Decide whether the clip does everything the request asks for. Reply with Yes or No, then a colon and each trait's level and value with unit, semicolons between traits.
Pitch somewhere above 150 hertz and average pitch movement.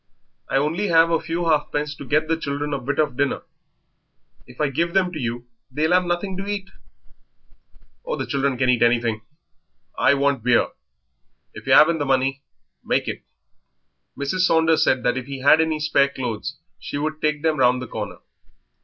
No: medium, 145 Hz; average, 3.7 semitones